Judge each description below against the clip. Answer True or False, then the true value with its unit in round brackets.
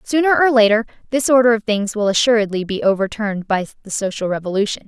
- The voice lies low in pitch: False (220 Hz)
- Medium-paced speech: True (185 wpm)